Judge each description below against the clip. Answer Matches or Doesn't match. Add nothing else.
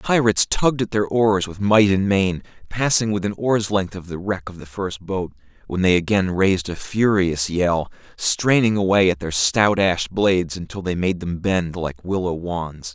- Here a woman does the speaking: Doesn't match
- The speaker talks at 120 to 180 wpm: Doesn't match